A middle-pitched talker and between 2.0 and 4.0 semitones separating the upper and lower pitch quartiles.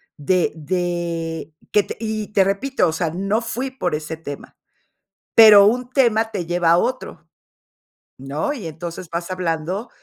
No: medium, 180 Hz; average, 5.0 semitones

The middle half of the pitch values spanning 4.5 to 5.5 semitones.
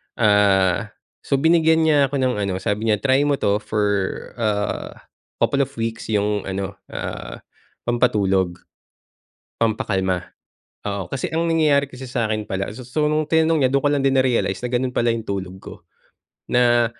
Yes: average, 5.1 semitones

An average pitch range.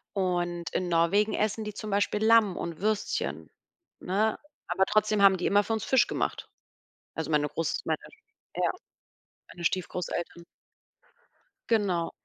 Yes: average, 3.6 semitones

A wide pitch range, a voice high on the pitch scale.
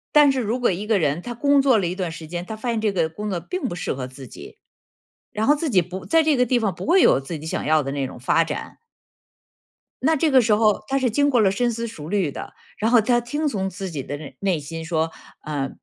Yes: wide, 7.2 semitones; high, 205 Hz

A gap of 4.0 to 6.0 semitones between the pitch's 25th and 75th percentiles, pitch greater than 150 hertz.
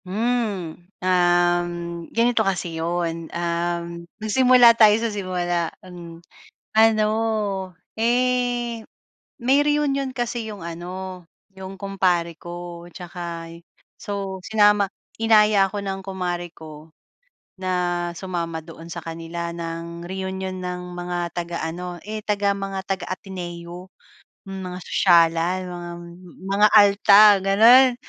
No: average, 3.3 semitones; medium, 185 Hz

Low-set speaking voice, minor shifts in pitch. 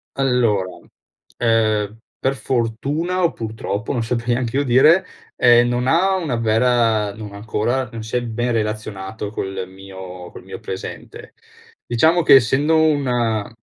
No: low, 115 Hz; average, 3.5 semitones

